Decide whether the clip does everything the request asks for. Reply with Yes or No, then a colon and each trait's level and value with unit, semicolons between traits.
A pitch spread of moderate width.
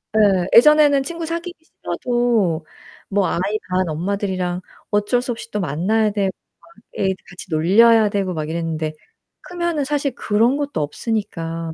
No: wide, 5.7 semitones